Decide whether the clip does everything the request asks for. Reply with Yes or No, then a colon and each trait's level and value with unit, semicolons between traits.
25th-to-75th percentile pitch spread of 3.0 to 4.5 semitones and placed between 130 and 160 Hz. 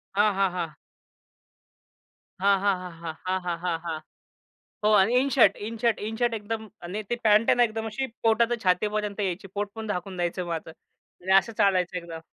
No: average, 3.6 semitones; high, 200 Hz